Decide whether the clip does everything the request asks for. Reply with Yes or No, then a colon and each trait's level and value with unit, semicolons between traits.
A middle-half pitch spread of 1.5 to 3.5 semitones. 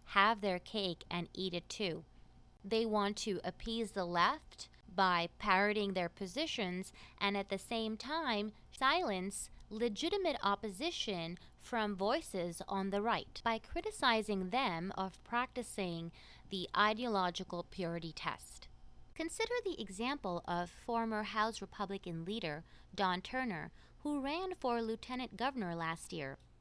No: average, 4.2 semitones